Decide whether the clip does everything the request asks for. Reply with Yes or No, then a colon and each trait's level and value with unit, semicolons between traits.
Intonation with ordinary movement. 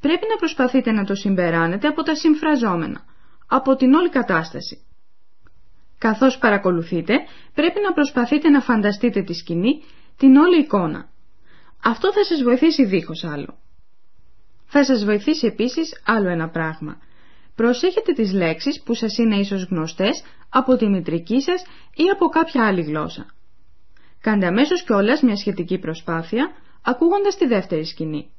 No: wide, 9.0 semitones